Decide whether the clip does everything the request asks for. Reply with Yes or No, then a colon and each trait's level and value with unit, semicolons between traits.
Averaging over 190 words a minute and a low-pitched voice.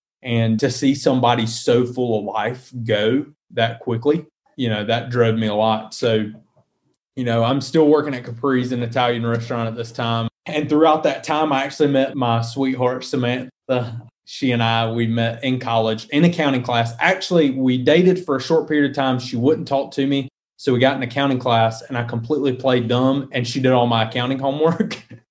Yes: average, 200 wpm; low, 125 Hz